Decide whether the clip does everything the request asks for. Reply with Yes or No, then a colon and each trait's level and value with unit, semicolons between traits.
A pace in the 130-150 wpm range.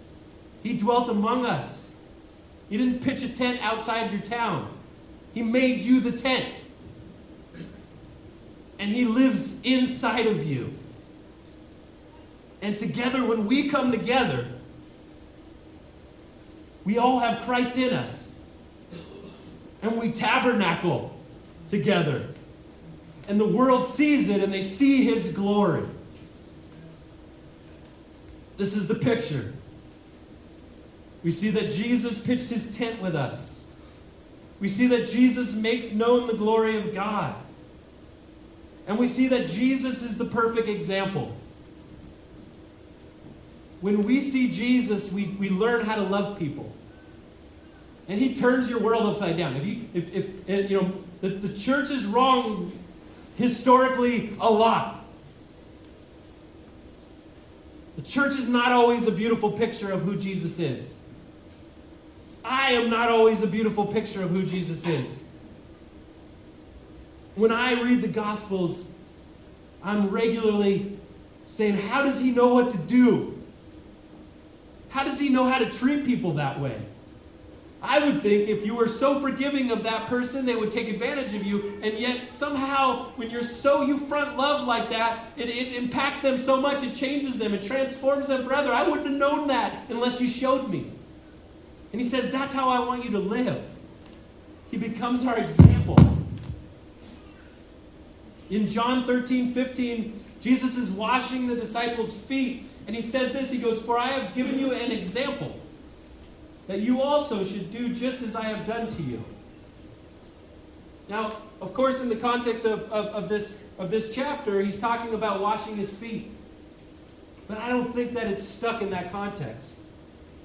Yes: average, 145 wpm